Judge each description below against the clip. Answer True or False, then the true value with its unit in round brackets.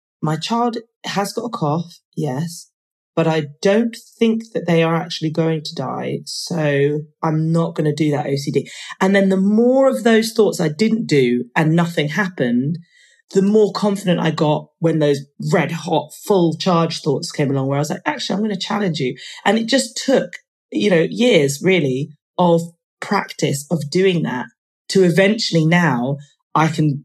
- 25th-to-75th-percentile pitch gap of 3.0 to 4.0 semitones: False (4.6 semitones)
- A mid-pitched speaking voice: True (165 Hz)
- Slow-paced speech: False (180 wpm)